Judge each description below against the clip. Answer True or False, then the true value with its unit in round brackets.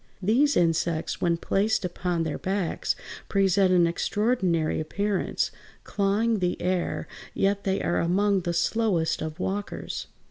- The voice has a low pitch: False (190 Hz)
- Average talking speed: False (130 wpm)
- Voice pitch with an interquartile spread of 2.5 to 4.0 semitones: True (3.0 semitones)